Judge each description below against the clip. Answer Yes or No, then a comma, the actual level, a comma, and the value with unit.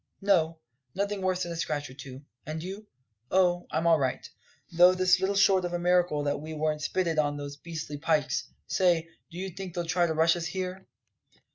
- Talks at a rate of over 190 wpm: Yes, fast, 205 wpm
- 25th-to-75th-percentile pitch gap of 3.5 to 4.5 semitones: No, average, 3.1 semitones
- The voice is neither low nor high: Yes, medium, 170 Hz